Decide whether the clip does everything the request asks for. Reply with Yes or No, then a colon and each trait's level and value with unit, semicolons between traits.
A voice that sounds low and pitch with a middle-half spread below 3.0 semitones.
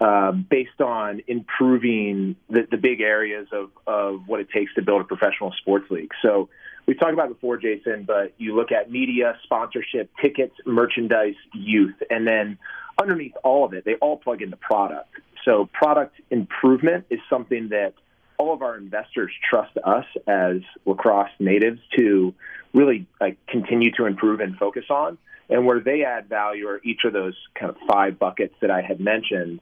No: low, 115 Hz; average, 3.5 semitones